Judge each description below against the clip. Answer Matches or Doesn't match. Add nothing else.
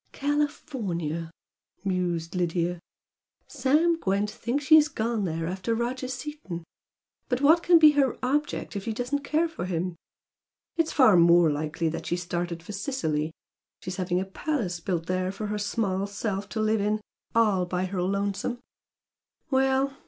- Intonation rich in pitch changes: Matches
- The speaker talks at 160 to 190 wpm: Doesn't match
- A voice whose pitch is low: Doesn't match